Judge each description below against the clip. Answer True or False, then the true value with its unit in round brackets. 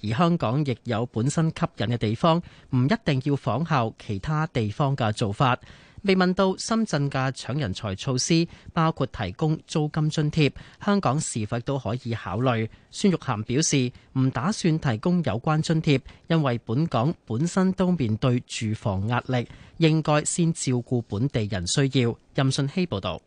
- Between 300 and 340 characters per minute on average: False (245 characters per minute)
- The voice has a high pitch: False (135 Hz)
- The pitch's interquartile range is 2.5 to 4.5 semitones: False (5.2 semitones)